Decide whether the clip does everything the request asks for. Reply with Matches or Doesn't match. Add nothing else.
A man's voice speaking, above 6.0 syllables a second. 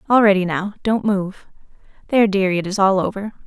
Doesn't match